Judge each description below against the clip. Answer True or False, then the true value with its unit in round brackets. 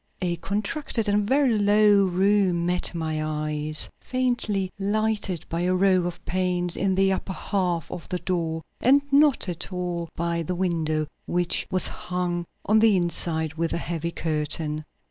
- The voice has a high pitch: False (180 Hz)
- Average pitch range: True (3.2 semitones)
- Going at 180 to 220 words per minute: False (160 wpm)